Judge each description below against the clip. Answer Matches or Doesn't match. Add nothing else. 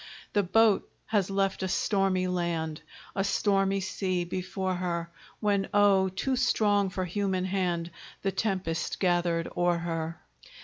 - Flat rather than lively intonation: Matches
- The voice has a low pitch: Doesn't match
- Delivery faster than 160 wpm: Doesn't match